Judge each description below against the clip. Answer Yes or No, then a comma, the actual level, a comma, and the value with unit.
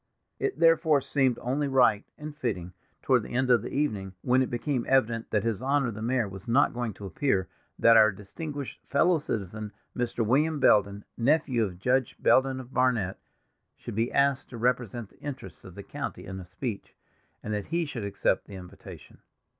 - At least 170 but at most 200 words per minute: Yes, average, 185 wpm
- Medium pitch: No, low, 120 Hz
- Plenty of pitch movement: No, average, 4.6 semitones